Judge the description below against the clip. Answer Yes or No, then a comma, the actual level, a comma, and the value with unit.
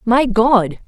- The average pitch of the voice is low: No, high, 230 Hz